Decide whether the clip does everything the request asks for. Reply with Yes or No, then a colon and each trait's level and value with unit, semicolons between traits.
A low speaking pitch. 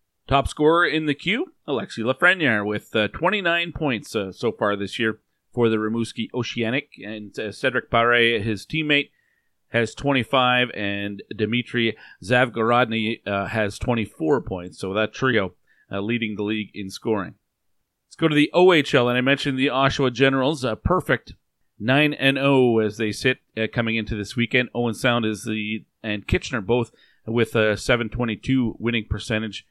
Yes: low, 115 Hz